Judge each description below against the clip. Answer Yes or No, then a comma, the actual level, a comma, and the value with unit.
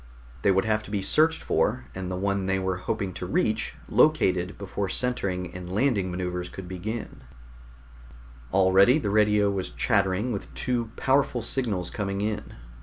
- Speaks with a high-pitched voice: No, low, 100 Hz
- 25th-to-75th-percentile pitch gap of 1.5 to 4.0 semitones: Yes, average, 3.1 semitones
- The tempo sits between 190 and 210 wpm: No, average, 170 wpm